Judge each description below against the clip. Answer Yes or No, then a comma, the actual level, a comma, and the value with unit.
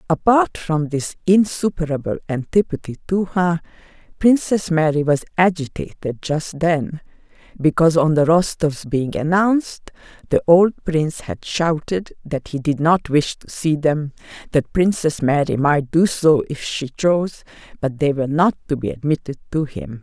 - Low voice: No, medium, 160 Hz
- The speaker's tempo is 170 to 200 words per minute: No, average, 150 wpm